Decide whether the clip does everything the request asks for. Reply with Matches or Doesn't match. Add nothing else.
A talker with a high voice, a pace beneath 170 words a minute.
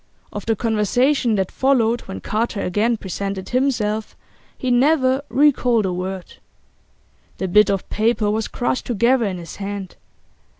Matches